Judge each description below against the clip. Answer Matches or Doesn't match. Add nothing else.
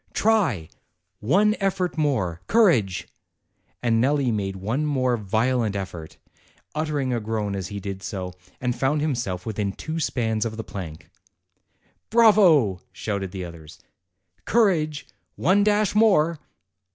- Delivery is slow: Matches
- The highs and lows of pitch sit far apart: Matches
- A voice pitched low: Matches